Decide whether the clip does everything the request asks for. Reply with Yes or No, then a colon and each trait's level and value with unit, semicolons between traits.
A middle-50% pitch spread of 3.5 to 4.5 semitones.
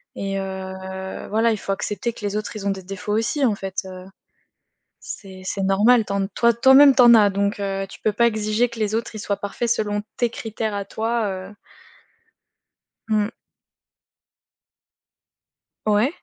No: average, 2.7 semitones